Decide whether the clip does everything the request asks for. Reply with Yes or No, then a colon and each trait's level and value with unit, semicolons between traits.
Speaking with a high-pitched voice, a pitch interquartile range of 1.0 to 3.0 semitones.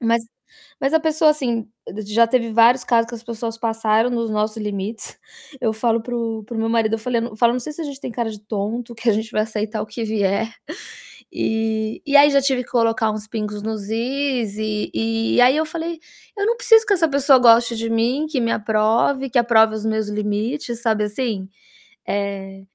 Yes: high, 230 Hz; narrow, 2.4 semitones